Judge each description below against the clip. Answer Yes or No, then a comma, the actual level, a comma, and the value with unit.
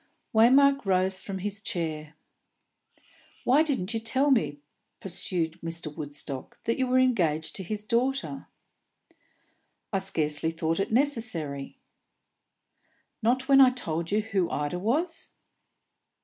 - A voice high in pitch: Yes, high, 195 Hz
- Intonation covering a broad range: Yes, wide, 7.6 semitones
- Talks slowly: Yes, slow, 120 wpm